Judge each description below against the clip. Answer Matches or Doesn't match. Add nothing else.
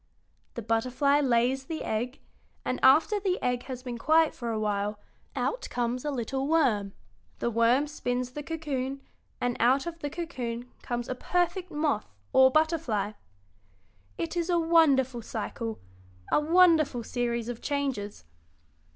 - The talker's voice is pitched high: Matches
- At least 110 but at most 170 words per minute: Matches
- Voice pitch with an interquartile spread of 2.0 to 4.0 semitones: Doesn't match